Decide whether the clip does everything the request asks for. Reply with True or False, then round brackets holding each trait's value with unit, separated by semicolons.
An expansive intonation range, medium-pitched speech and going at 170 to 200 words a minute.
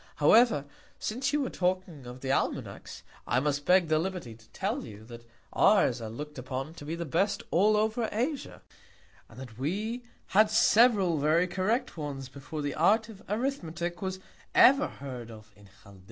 True (8.0 semitones; 170 Hz; 175 wpm)